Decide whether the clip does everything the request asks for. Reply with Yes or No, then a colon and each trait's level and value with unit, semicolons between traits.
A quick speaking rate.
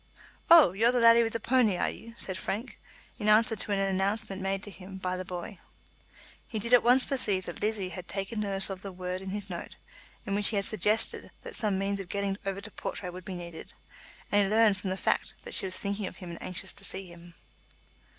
Yes: fast, 235 wpm